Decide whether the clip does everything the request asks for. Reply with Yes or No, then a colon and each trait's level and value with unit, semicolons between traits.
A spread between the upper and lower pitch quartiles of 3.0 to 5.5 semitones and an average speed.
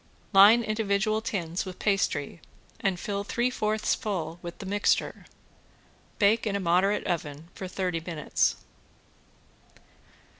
No: average, 3.6 semitones; slow, 120 wpm